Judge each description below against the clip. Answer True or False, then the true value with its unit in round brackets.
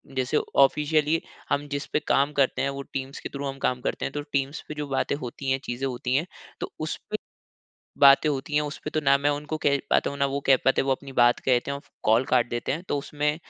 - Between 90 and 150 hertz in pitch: True (140 Hz)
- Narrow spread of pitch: True (1.7 semitones)